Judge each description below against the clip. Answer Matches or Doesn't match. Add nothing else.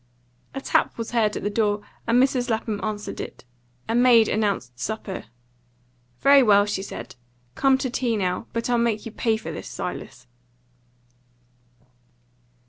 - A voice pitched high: Matches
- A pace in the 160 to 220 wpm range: Doesn't match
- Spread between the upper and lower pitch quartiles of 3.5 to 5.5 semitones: Doesn't match